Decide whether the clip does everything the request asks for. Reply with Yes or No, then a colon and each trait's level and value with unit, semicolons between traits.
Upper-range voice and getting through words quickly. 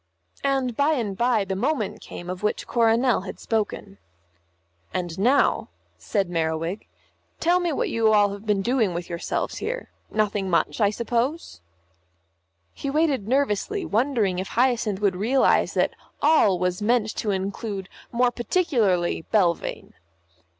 No: high, 215 Hz; average, 140 wpm